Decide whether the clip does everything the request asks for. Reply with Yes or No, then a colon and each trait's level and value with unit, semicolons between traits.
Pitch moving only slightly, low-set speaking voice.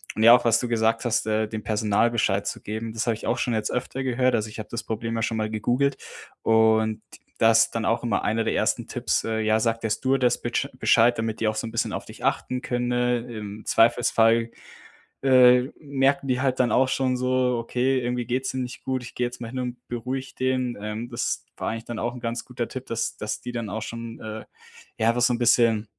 Yes: narrow, 2.0 semitones; low, 115 Hz